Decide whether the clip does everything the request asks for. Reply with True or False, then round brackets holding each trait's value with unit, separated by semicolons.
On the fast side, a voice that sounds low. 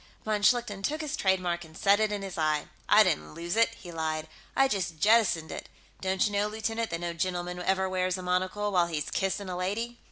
False (220 wpm; 190 Hz)